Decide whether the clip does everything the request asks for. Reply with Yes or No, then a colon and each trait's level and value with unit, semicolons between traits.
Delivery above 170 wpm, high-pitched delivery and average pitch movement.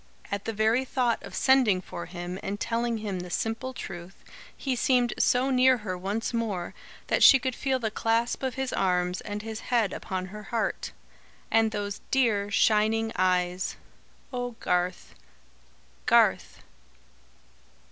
No: average, 145 wpm; high, 220 Hz; average, 4.4 semitones